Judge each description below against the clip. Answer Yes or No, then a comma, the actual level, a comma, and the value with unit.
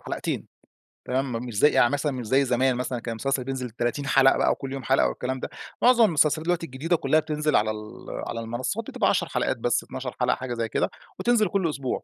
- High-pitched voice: No, low, 130 Hz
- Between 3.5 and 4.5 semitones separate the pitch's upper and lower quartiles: Yes, average, 3.9 semitones